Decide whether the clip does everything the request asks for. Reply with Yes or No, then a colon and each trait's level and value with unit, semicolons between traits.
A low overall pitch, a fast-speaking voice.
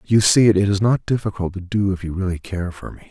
Yes: very low, 95 Hz; fast, 270 wpm